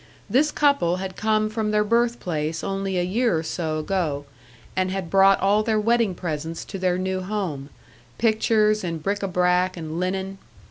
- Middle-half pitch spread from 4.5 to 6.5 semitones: No, average, 3.3 semitones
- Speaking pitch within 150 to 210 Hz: Yes, high, 190 Hz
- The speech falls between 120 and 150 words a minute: No, average, 180 wpm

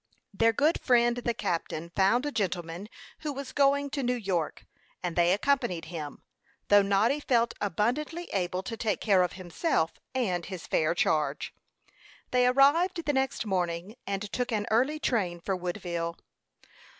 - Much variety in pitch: Yes, wide, 6.4 semitones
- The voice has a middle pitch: No, high, 210 Hz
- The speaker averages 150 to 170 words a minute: Yes, average, 155 wpm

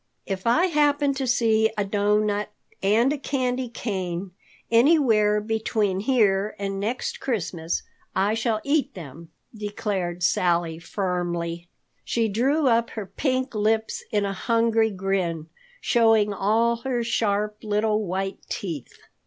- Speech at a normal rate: No, slow, 130 wpm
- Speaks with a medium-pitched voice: No, high, 210 Hz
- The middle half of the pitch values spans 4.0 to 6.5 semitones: No, average, 3.3 semitones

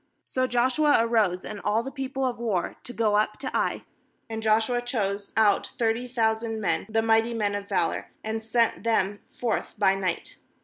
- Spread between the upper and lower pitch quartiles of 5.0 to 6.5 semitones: No, narrow, 2.5 semitones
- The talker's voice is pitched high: Yes, high, 225 Hz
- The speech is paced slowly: No, average, 180 wpm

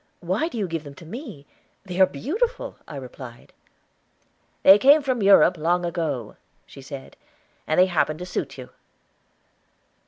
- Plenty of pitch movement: Yes, wide, 6.4 semitones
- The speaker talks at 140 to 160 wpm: Yes, average, 155 wpm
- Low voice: No, medium, 175 Hz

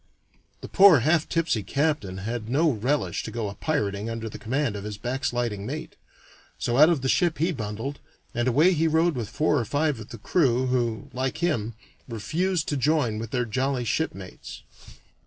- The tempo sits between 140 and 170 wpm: No, average, 185 wpm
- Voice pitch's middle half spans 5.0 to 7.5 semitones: Yes, wide, 5.5 semitones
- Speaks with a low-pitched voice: Yes, low, 130 Hz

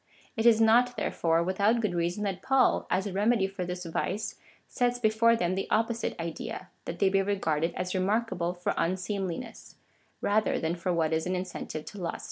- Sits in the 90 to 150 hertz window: No, high, 190 Hz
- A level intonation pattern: No, average, 4.0 semitones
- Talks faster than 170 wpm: Yes, average, 190 wpm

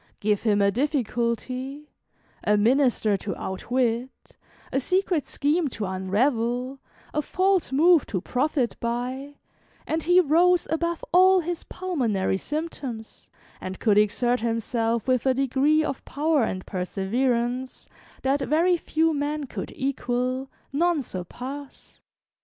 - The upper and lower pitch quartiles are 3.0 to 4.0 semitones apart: No, average, 4.8 semitones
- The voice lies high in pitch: Yes, very high, 260 Hz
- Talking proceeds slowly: Yes, slow, 125 wpm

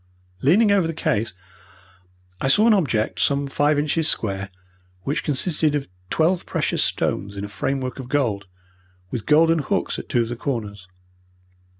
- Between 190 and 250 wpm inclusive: No, average, 160 wpm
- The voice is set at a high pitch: No, medium, 140 Hz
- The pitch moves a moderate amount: No, wide, 6.0 semitones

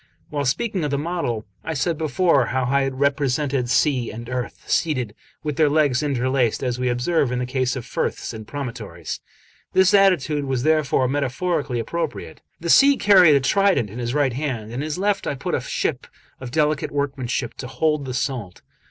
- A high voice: No, medium, 140 Hz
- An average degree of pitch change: Yes, average, 3.7 semitones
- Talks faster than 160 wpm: Yes, average, 190 wpm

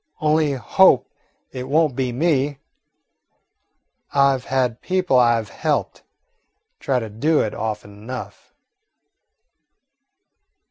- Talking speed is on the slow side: Yes, slow, 105 wpm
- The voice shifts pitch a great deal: No, average, 3.8 semitones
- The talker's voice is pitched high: No, low, 130 Hz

